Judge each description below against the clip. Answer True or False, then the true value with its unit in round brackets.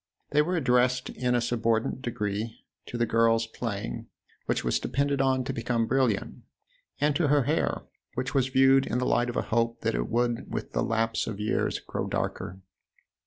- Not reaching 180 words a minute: False (190 wpm)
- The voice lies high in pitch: False (120 Hz)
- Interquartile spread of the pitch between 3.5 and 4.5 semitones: False (2.5 semitones)